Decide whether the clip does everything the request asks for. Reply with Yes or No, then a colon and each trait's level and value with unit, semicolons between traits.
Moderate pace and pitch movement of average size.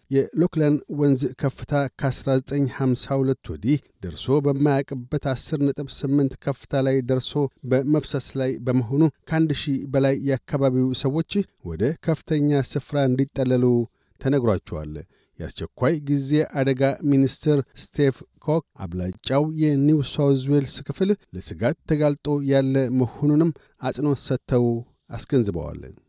No: average, 100 wpm; narrow, 2.2 semitones